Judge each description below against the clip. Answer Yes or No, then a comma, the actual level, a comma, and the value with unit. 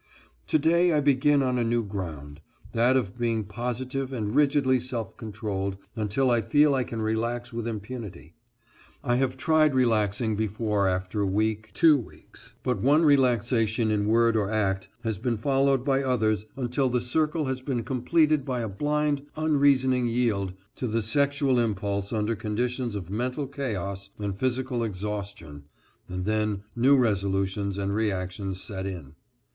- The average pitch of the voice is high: No, low, 115 Hz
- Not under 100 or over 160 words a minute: Yes, average, 155 wpm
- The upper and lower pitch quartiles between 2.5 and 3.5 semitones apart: No, average, 4.3 semitones